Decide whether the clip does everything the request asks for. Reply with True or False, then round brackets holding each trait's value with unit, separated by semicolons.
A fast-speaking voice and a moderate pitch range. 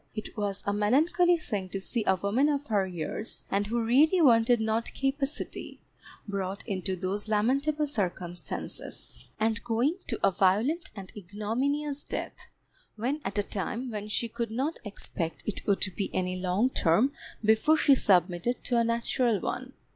False (160 wpm; 5.0 semitones)